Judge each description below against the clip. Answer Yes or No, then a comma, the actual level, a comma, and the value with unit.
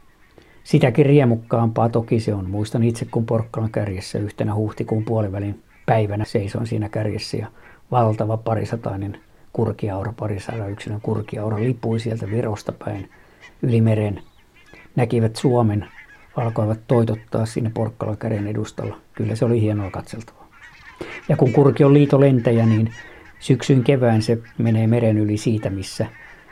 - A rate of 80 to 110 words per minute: No, average, 130 wpm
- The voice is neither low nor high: No, low, 115 Hz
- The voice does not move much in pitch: Yes, narrow, 1.8 semitones